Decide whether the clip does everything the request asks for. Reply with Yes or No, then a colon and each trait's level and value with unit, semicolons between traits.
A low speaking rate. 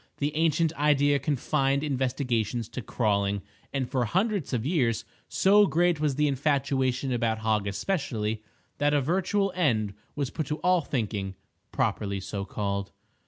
No: average, 145 wpm